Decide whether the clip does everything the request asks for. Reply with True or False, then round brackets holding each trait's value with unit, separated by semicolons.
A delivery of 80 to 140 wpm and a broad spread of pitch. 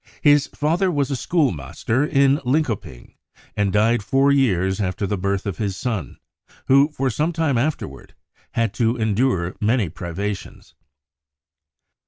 True (135 wpm; 6.1 semitones)